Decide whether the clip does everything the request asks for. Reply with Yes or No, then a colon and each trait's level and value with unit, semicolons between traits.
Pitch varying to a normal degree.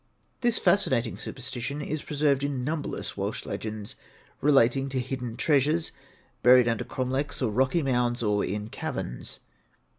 Yes: average, 3.3 semitones